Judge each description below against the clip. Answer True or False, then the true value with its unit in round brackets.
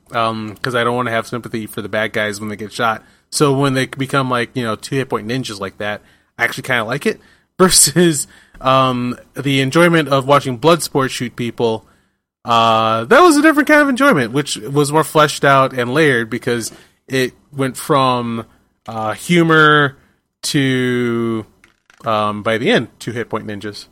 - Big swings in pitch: False (4.2 semitones)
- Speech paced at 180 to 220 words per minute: True (190 wpm)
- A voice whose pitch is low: True (125 Hz)